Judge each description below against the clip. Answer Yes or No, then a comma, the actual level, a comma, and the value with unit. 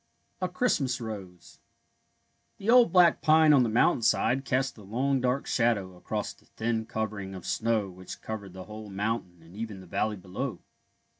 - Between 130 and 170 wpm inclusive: Yes, average, 165 wpm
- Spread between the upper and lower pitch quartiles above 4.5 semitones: Yes, average, 5.2 semitones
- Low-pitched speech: Yes, low, 110 Hz